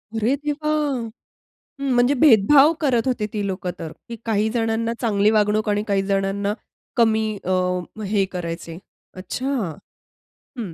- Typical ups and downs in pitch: Yes, average, 3.3 semitones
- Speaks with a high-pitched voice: Yes, high, 215 Hz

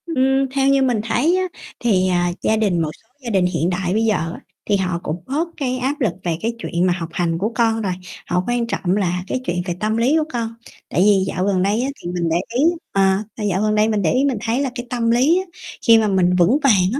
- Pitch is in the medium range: No, high, 215 Hz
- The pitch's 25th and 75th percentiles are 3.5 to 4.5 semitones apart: No, average, 5.2 semitones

